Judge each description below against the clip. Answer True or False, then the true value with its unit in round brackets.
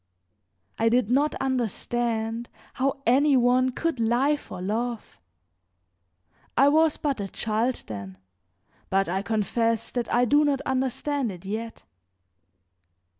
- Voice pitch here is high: True (240 Hz)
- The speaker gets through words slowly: True (125 wpm)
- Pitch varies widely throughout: False (3.4 semitones)